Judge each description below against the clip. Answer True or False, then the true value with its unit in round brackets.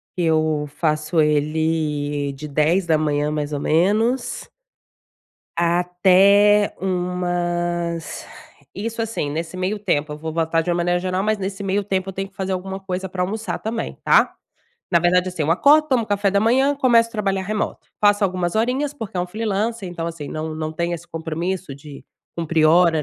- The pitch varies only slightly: False (3.9 semitones)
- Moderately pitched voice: True (180 Hz)